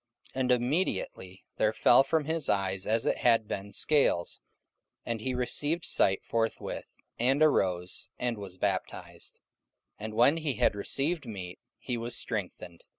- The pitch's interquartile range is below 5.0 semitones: No, wide, 5.6 semitones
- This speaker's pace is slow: No, average, 150 wpm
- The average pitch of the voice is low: Yes, low, 115 Hz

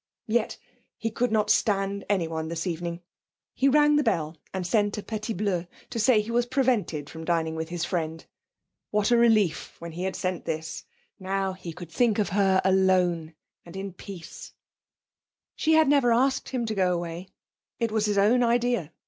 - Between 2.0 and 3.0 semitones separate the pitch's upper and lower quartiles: No, average, 5.0 semitones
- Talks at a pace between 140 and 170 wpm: No, average, 180 wpm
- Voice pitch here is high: Yes, high, 195 Hz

